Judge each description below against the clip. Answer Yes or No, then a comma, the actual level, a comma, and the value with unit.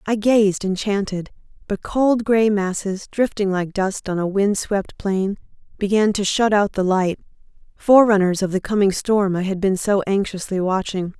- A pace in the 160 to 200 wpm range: Yes, average, 170 wpm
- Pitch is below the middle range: No, high, 200 Hz